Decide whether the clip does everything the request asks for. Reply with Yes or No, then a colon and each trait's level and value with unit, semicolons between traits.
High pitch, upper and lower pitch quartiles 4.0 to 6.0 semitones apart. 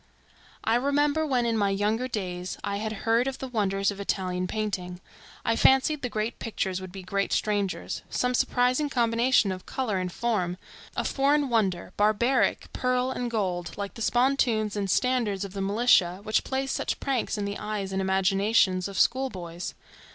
Yes: high, 215 Hz; average, 4.4 semitones